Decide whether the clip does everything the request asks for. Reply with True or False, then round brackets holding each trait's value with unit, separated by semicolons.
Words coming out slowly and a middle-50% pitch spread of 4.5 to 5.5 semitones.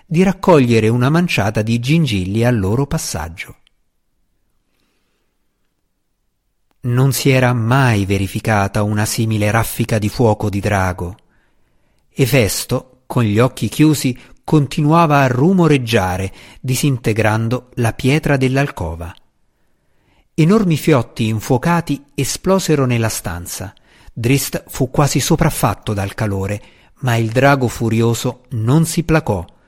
True (105 wpm; 4.9 semitones)